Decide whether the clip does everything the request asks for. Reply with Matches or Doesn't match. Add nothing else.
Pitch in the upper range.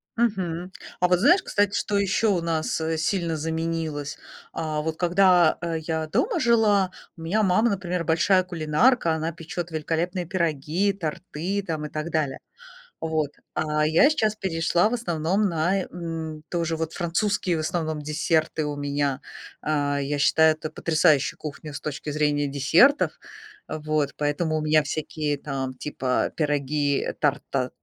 Doesn't match